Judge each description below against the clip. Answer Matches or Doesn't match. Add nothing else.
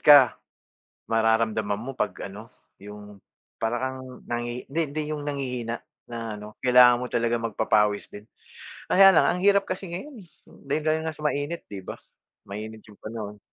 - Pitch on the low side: Matches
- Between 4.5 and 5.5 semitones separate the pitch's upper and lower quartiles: Matches